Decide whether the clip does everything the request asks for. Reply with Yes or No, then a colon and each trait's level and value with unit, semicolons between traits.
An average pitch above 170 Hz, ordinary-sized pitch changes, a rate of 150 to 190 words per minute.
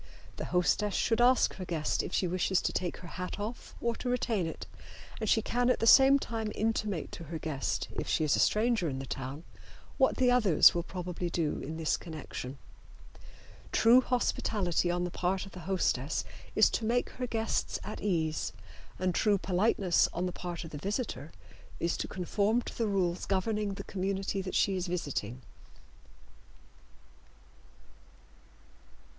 Yes: medium, 185 Hz; average, 4.5 semitones; average, 170 wpm